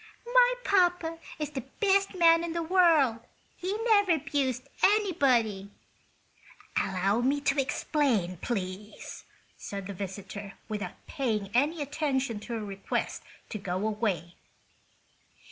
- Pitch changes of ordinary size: No, wide, 8.4 semitones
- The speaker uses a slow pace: Yes, slow, 120 wpm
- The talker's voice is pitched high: Yes, very high, 265 Hz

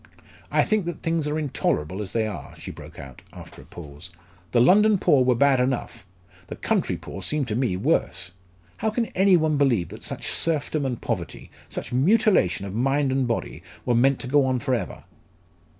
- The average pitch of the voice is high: No, low, 130 Hz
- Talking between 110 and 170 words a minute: No, average, 195 wpm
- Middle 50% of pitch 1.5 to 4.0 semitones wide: No, wide, 5.5 semitones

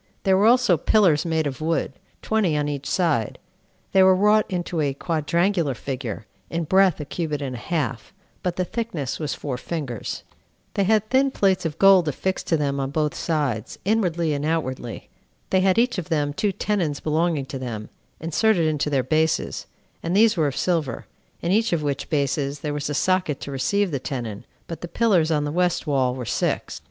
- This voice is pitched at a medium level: Yes, medium, 160 Hz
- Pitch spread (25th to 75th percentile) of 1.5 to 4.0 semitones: No, average, 4.7 semitones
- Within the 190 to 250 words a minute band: Yes, average, 195 wpm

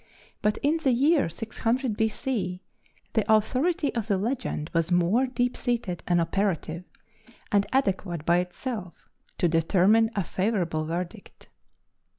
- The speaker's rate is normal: No, slow, 130 wpm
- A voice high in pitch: Yes, high, 205 Hz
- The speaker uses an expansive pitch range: Yes, wide, 5.7 semitones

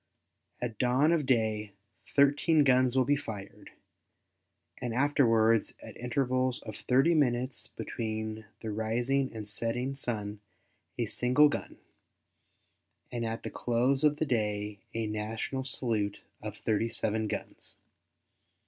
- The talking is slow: Yes, slow, 125 wpm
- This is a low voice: Yes, low, 120 Hz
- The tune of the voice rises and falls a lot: No, average, 3.3 semitones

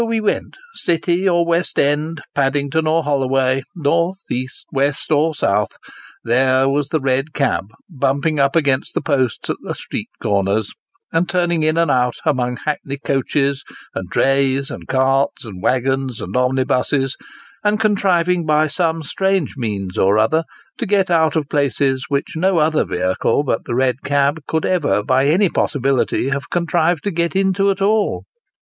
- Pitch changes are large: No, average, 4.1 semitones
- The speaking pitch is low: No, medium, 145 Hz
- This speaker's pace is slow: No, average, 165 wpm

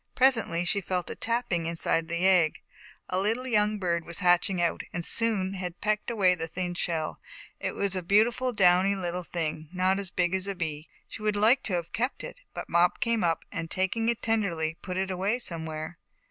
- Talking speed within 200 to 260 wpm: Yes, fast, 205 wpm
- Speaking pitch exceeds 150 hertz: Yes, medium, 185 Hz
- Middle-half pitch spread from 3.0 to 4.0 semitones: Yes, average, 3.7 semitones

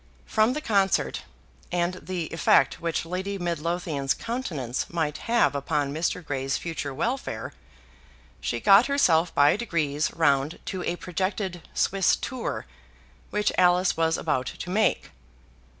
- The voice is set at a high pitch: No, medium, 175 Hz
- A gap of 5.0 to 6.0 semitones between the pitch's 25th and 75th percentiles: No, average, 4.6 semitones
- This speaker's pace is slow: Yes, slow, 130 wpm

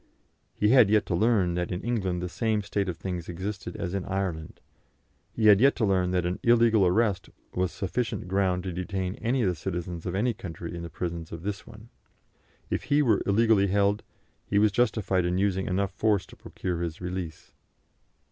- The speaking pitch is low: Yes, very low, 95 Hz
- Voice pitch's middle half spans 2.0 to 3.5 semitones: Yes, average, 3.0 semitones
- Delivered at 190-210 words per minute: Yes, average, 195 wpm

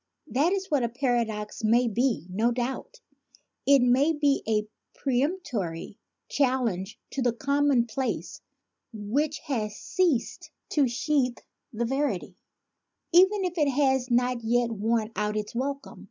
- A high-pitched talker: Yes, very high, 250 Hz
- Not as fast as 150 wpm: Yes, slow, 135 wpm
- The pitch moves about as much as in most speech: Yes, average, 3.9 semitones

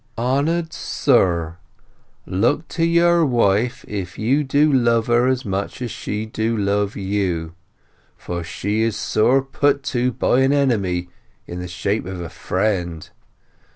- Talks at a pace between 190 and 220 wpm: No, average, 145 wpm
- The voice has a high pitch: No, low, 110 Hz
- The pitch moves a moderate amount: No, wide, 5.9 semitones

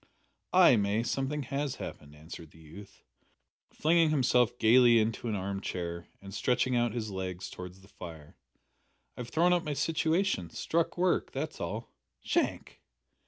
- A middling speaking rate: Yes, average, 155 wpm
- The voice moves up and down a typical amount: No, wide, 7.6 semitones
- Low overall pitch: Yes, low, 115 Hz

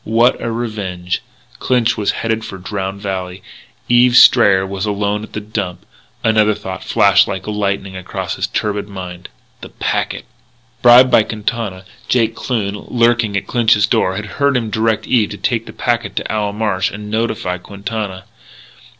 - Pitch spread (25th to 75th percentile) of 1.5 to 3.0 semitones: Yes, average, 2.7 semitones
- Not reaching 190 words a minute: Yes, average, 165 wpm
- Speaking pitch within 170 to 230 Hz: No, low, 105 Hz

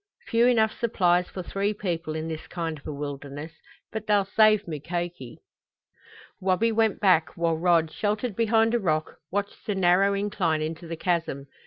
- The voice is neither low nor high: Yes, medium, 180 Hz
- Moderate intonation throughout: Yes, average, 4.5 semitones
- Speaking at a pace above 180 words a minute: No, average, 165 wpm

